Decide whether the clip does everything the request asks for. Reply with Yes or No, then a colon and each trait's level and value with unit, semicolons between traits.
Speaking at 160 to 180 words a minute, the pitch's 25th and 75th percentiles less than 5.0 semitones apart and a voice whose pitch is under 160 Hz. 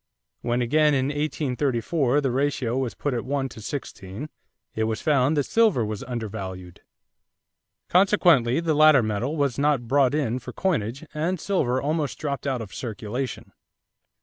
No: average, 150 wpm; average, 4.1 semitones; low, 135 Hz